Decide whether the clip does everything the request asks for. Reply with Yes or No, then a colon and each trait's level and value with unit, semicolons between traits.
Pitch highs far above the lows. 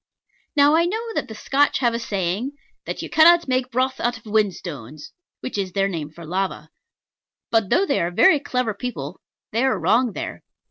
Yes: wide, 6.3 semitones